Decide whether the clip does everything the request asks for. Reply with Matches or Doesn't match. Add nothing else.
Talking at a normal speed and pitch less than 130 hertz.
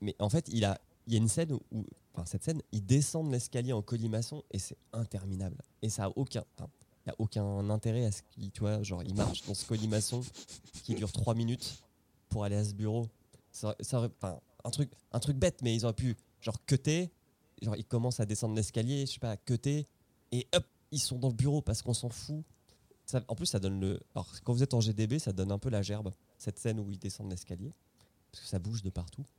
Doesn't match